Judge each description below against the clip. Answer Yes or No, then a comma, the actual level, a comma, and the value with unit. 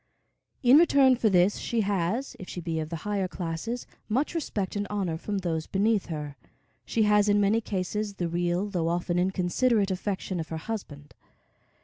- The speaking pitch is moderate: No, high, 195 Hz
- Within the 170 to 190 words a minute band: Yes, average, 175 wpm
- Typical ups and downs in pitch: Yes, average, 3.7 semitones